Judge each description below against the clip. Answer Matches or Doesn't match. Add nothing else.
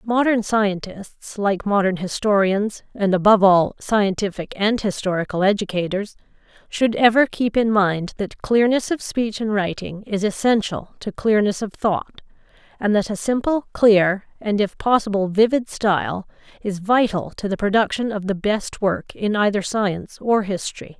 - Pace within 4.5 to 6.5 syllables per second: Matches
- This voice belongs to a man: Doesn't match